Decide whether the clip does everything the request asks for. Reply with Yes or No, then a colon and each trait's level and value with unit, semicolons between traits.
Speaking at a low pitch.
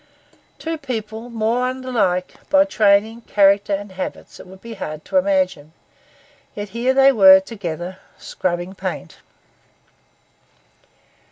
No: high, 210 Hz